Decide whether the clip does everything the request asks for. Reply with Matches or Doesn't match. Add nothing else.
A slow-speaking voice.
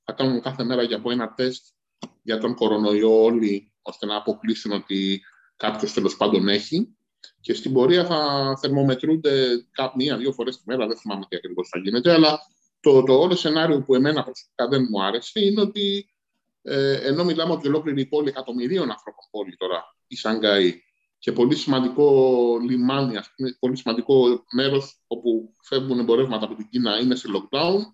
Doesn't match